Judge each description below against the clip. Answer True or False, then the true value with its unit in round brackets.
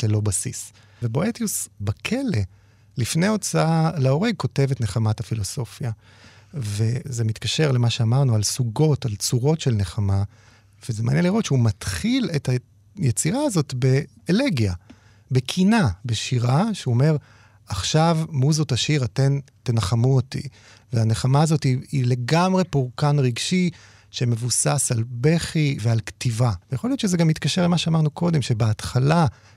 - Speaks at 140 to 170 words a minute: False (125 wpm)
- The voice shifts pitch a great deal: True (5.7 semitones)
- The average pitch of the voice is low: True (125 Hz)